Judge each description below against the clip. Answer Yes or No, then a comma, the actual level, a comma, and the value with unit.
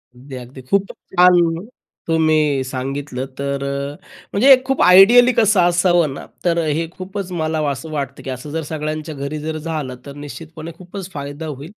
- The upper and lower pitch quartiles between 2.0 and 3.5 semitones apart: No, average, 4.1 semitones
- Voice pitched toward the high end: No, medium, 155 Hz